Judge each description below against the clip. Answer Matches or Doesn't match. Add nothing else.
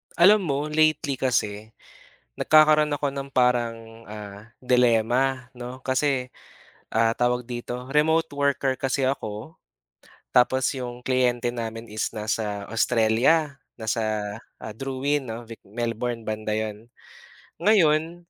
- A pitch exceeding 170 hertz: Doesn't match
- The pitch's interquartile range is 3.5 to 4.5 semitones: Matches